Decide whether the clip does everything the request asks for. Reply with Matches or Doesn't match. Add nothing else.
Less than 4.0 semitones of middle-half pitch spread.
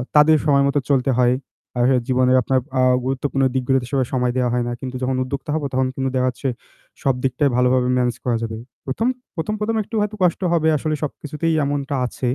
Matches